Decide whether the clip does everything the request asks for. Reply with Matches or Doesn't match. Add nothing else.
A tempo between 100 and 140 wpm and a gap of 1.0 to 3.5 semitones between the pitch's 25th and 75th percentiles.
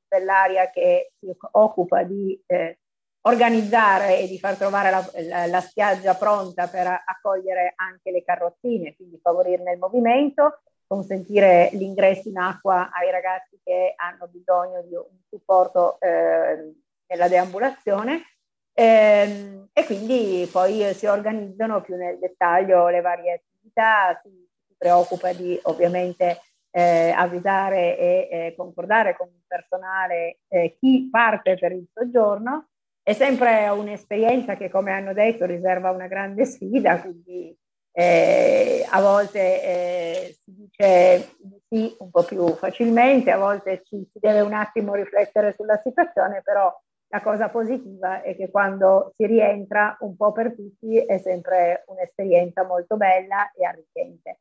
Matches